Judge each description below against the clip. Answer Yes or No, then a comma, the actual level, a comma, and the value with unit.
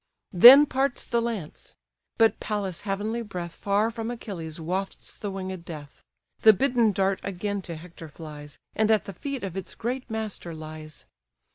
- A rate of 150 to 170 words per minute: Yes, average, 160 wpm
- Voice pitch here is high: Yes, high, 195 Hz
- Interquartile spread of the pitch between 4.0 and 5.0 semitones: Yes, average, 4.7 semitones